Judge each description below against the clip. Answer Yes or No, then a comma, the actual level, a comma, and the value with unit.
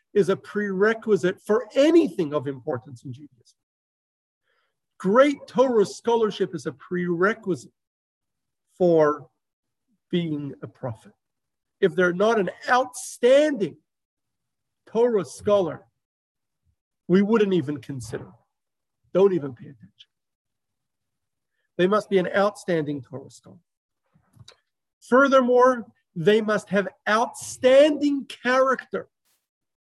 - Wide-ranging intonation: Yes, wide, 7.4 semitones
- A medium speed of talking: No, slow, 95 wpm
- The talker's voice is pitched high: Yes, high, 195 Hz